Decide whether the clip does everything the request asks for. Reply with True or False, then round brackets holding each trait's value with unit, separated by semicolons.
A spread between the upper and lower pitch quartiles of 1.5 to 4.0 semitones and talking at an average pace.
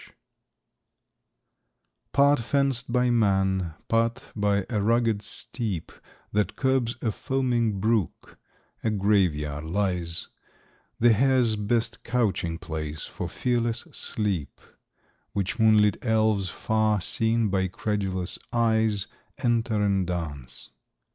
False (3.6 semitones; 110 wpm)